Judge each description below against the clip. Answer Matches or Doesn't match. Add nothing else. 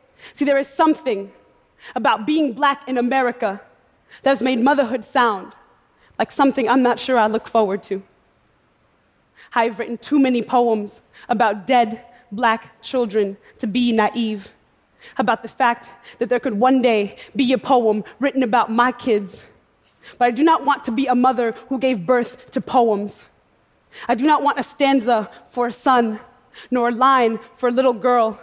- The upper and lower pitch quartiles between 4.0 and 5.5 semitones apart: Doesn't match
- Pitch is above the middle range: Matches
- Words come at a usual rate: Matches